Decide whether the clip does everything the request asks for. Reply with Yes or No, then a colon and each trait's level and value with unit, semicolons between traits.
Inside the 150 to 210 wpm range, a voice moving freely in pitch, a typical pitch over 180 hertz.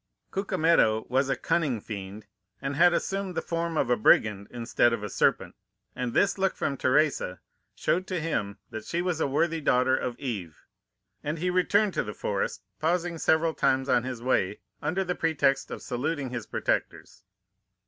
No: average, 175 wpm; wide, 6.1 semitones; medium, 140 Hz